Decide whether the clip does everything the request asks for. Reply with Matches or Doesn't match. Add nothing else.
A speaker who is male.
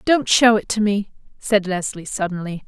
Doesn't match